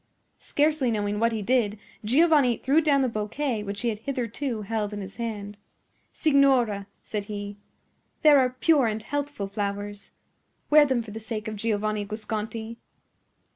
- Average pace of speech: Yes, average, 155 wpm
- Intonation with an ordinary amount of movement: Yes, average, 4.2 semitones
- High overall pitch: Yes, high, 225 Hz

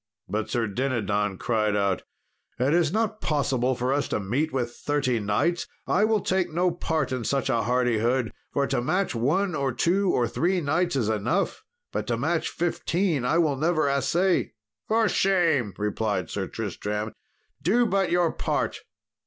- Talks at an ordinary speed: Yes, average, 165 wpm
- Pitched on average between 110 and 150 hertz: Yes, medium, 140 Hz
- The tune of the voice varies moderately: No, wide, 6.9 semitones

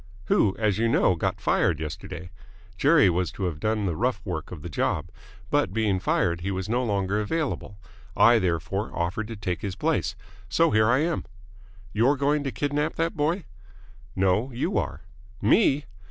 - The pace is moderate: Yes, average, 175 wpm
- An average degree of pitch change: No, wide, 6.5 semitones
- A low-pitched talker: Yes, low, 105 Hz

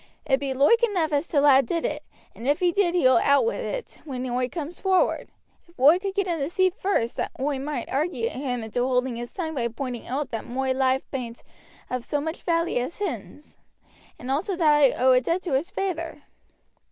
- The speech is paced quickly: Yes, fast, 215 wpm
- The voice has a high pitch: Yes, very high, 285 Hz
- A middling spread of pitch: Yes, average, 5.0 semitones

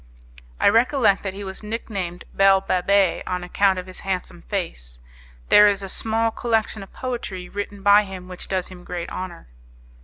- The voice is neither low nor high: No, high, 195 Hz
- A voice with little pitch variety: Yes, narrow, 2.3 semitones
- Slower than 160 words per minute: No, average, 175 wpm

